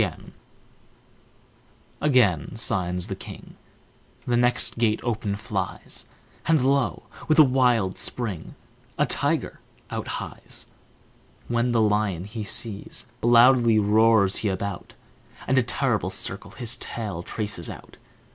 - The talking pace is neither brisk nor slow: No, slow, 120 wpm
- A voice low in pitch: Yes, low, 110 Hz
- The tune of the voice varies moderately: Yes, average, 3.4 semitones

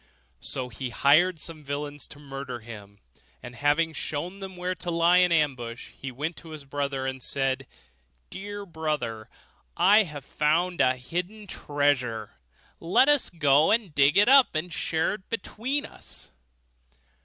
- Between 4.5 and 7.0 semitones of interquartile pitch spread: Yes, average, 5.0 semitones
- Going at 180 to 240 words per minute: No, average, 155 wpm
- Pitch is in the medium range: Yes, medium, 150 Hz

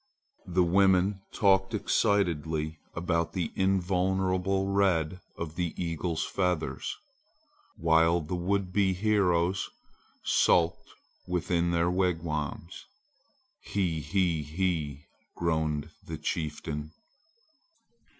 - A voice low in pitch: Yes, very low, 90 Hz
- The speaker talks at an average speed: No, slow, 90 wpm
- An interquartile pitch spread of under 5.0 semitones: Yes, average, 2.7 semitones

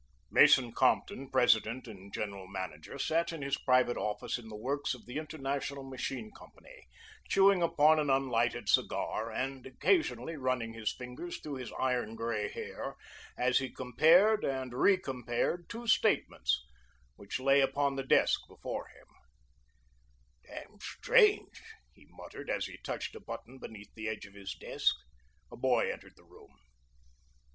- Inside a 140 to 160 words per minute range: Yes, average, 150 wpm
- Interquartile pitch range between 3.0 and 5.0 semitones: Yes, average, 4.3 semitones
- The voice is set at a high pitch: No, low, 130 Hz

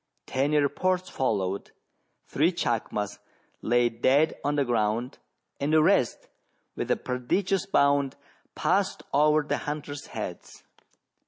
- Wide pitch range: No, average, 4.1 semitones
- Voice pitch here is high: No, medium, 140 Hz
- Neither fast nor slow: No, slow, 115 wpm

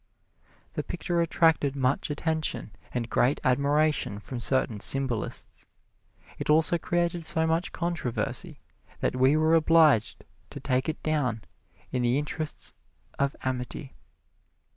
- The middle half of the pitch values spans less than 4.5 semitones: Yes, average, 4.1 semitones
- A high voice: No, medium, 145 Hz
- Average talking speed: No, slow, 120 wpm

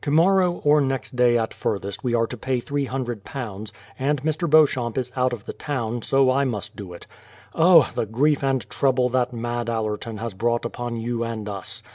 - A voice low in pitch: Yes, low, 120 Hz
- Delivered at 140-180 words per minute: No, average, 195 wpm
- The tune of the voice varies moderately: Yes, average, 3.2 semitones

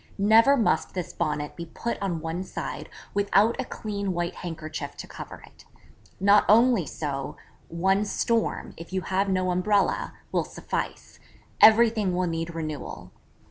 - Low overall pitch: No, medium, 185 Hz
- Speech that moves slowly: No, average, 145 wpm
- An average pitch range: Yes, average, 4.0 semitones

